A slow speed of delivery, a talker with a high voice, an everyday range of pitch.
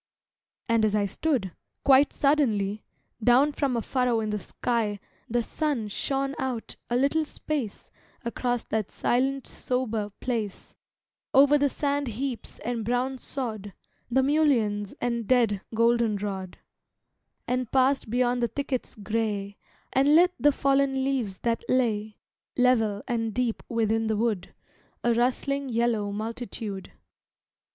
Yes: slow, 130 wpm; high, 240 Hz; average, 3.7 semitones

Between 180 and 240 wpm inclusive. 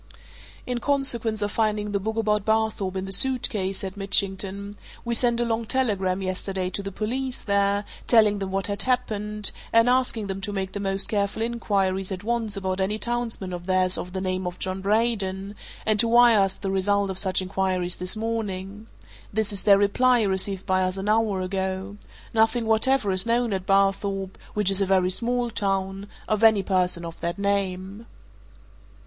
Yes: average, 185 wpm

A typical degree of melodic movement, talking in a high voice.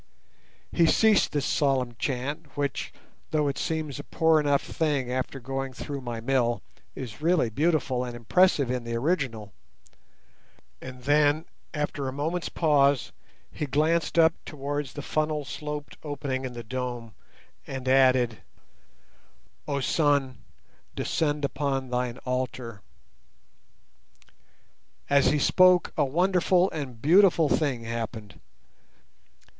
No: average, 3.2 semitones; medium, 140 Hz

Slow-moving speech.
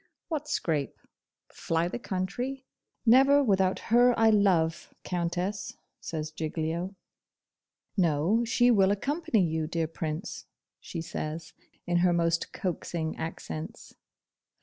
Yes: slow, 110 wpm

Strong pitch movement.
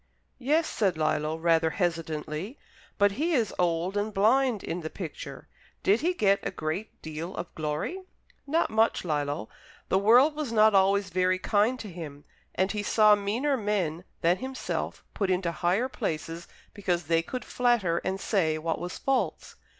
No: average, 5.0 semitones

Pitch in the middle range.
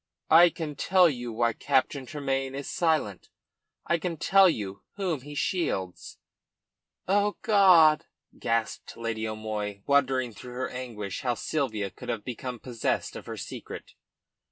No: low, 130 Hz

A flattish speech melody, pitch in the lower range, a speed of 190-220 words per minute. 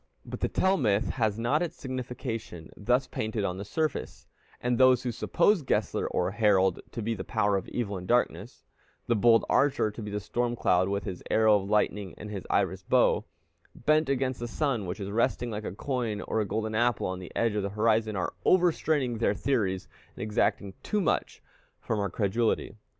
No: average, 3.4 semitones; low, 110 Hz; average, 200 wpm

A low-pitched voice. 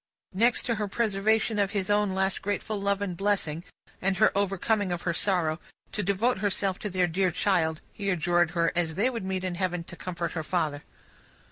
No: high, 190 Hz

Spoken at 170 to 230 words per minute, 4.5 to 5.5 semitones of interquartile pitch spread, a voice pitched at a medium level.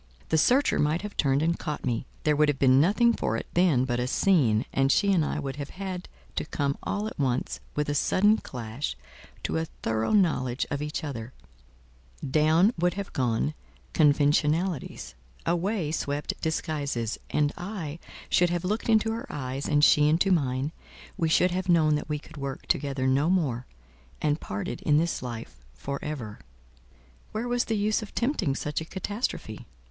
Yes: average, 175 wpm; average, 5.1 semitones; medium, 150 Hz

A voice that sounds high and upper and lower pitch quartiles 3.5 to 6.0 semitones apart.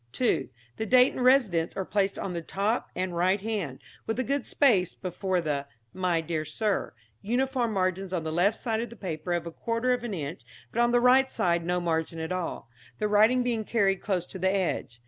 Yes: high, 195 Hz; average, 5.2 semitones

